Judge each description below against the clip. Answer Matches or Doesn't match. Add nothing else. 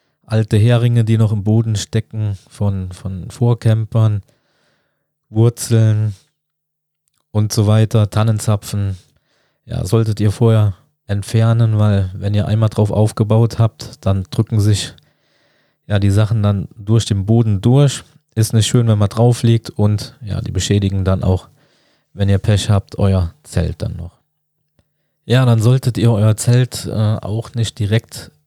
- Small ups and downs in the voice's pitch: Matches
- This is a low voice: Matches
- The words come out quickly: Doesn't match